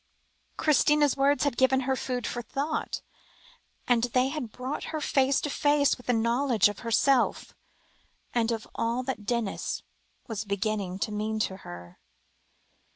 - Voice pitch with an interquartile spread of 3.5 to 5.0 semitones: Yes, average, 3.8 semitones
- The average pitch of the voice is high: Yes, high, 245 Hz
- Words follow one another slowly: No, average, 155 wpm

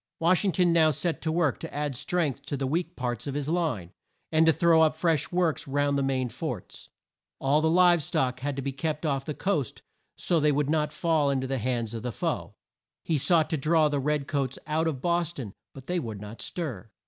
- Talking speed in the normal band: No, fast, 235 wpm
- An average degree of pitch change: Yes, average, 3.5 semitones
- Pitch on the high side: No, medium, 150 Hz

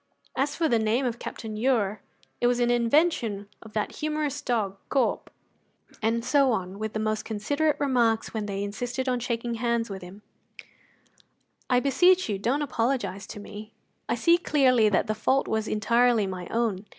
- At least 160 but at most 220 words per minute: Yes, average, 170 wpm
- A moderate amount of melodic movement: Yes, average, 3.5 semitones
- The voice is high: Yes, high, 230 Hz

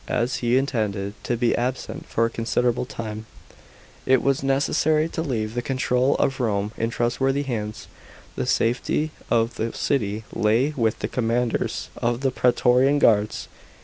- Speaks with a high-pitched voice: No, low, 120 Hz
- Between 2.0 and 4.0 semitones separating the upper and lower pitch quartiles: Yes, average, 2.9 semitones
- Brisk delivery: No, average, 150 wpm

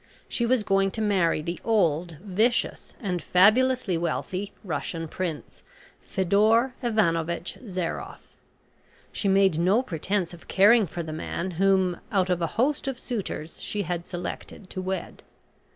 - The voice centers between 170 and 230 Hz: Yes, high, 190 Hz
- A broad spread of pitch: No, average, 3.7 semitones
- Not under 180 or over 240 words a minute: No, average, 140 wpm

